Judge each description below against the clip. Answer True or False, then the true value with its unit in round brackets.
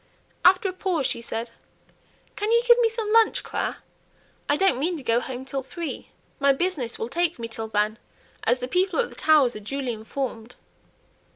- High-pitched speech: True (275 Hz)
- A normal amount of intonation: False (7.8 semitones)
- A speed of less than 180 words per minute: False (190 wpm)